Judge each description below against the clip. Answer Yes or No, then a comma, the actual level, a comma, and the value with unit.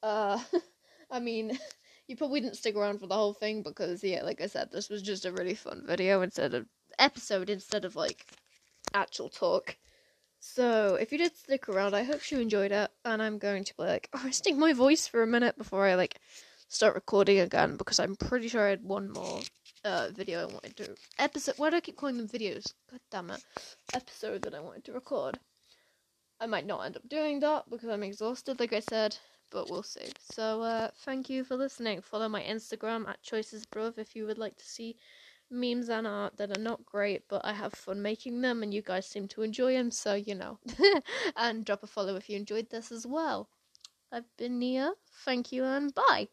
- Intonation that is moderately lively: Yes, average, 4.1 semitones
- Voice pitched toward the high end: Yes, high, 225 Hz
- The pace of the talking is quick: Yes, fast, 215 wpm